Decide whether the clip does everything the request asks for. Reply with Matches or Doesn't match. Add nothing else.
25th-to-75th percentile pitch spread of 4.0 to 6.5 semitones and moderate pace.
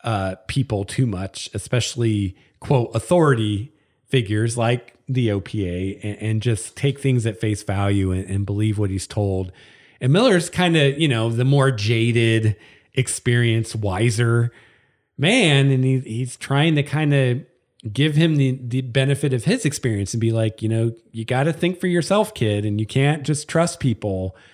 Matches